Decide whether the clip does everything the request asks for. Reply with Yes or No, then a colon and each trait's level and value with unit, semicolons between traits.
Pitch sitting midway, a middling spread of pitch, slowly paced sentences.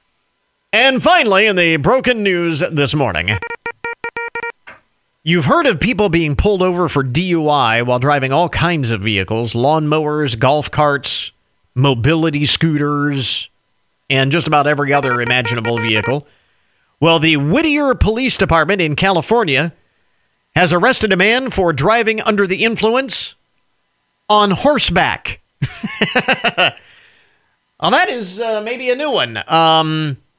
No: medium, 165 Hz; wide, 7.2 semitones; slow, 125 wpm